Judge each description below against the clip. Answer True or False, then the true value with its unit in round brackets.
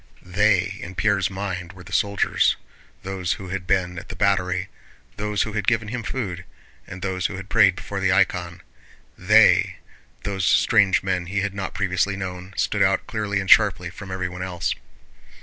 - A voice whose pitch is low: True (95 Hz)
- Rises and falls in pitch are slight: True (1.8 semitones)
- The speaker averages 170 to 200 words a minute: True (175 wpm)